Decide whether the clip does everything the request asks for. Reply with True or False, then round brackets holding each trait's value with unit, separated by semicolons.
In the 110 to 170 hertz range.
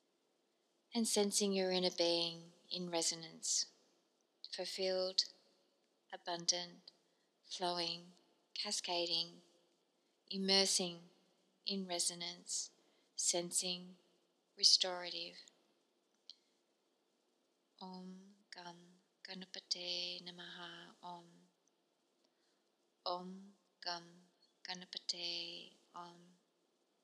False (180 Hz)